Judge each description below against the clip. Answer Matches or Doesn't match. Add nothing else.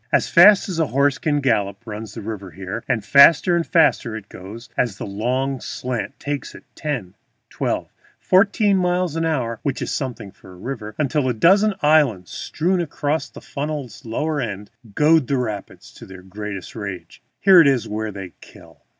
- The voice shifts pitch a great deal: Matches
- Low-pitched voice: Matches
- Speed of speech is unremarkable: Matches